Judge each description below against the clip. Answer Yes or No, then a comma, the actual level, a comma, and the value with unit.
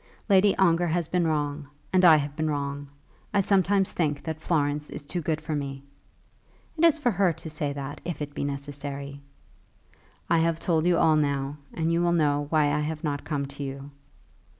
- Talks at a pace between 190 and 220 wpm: Yes, average, 195 wpm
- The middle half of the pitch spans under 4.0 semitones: Yes, average, 3.0 semitones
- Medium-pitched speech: Yes, medium, 155 Hz